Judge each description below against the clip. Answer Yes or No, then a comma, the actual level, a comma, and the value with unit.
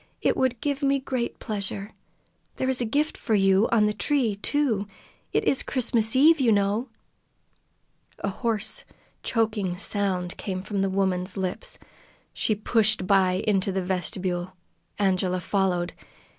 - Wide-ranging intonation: No, average, 3.8 semitones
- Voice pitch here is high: Yes, high, 205 Hz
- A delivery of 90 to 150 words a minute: Yes, average, 145 wpm